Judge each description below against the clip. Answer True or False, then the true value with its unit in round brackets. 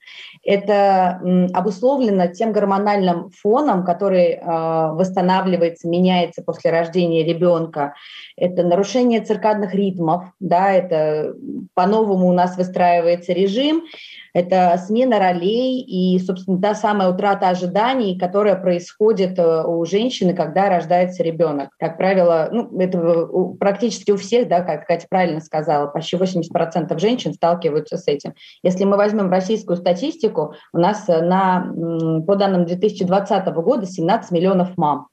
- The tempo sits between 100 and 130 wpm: True (120 wpm)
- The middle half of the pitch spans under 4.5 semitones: True (2.8 semitones)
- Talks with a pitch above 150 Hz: True (185 Hz)